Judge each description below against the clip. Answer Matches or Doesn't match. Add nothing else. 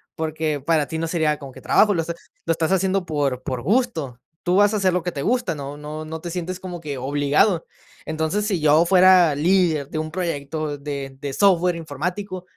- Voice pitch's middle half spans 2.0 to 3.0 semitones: Doesn't match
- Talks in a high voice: Doesn't match